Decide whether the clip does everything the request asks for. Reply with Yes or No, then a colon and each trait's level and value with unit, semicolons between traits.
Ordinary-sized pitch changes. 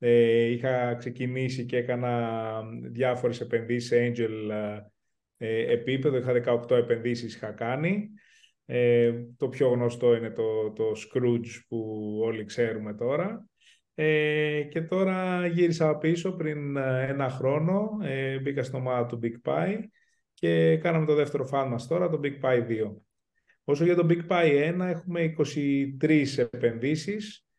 Yes: average, 4.8 semitones